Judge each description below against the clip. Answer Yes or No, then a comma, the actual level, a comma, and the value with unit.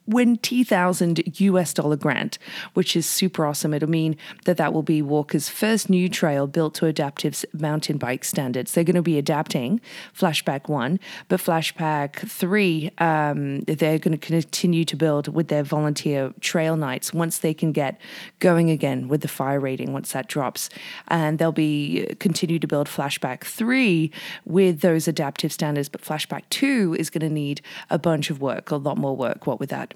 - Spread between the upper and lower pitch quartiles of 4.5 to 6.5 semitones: No, average, 3.2 semitones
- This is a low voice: No, medium, 160 Hz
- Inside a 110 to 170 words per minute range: No, average, 180 wpm